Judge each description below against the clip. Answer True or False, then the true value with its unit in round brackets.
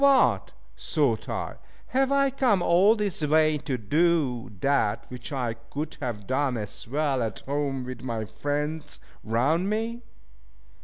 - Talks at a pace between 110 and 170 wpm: True (145 wpm)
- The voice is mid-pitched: True (145 Hz)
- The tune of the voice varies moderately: False (5.8 semitones)